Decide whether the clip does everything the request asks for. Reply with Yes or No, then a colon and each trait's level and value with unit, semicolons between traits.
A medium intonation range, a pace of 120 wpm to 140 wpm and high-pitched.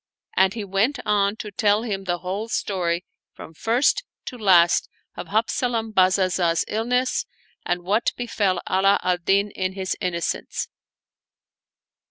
Yes: average, 3.0 semitones; slow, 135 wpm; high, 195 Hz